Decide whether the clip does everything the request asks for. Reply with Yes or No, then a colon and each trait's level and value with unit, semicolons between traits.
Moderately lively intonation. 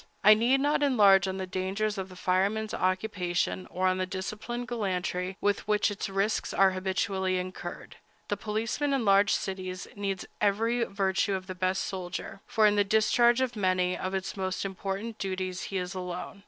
No: narrow, 2.3 semitones